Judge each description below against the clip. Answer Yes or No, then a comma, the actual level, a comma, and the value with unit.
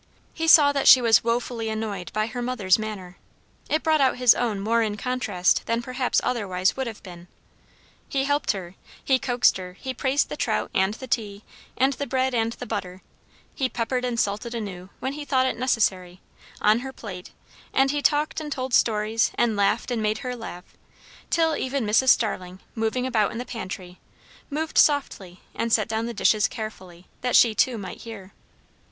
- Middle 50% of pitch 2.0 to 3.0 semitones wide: No, average, 4.2 semitones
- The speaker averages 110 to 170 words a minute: No, average, 190 wpm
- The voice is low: No, high, 230 Hz